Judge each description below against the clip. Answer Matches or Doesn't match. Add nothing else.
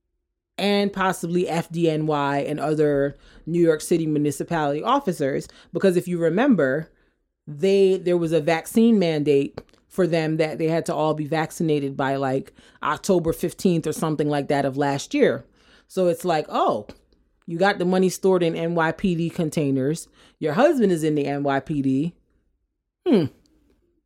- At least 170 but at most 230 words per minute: Doesn't match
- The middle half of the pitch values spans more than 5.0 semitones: Doesn't match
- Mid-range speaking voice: Matches